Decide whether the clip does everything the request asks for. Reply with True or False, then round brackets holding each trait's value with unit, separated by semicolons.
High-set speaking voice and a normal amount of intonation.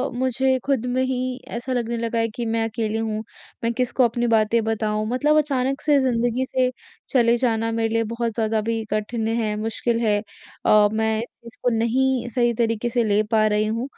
False (230 Hz; 2.2 semitones)